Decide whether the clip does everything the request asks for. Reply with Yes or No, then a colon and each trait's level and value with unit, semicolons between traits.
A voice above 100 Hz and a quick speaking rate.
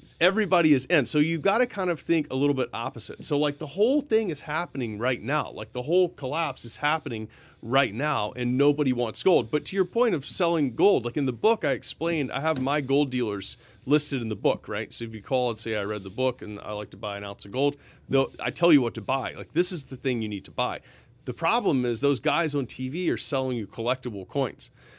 Yes: low, 135 Hz; fast, 250 wpm